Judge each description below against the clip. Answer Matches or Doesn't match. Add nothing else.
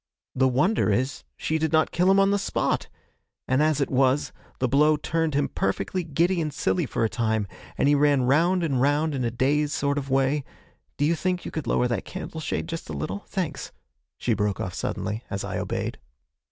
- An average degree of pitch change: Matches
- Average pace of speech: Doesn't match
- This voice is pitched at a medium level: Matches